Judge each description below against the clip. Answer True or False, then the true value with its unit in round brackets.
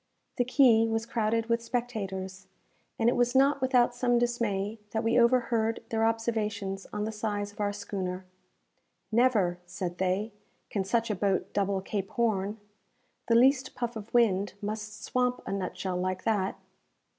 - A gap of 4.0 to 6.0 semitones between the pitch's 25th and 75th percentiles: False (3.2 semitones)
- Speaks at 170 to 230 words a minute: False (155 wpm)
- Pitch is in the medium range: False (220 Hz)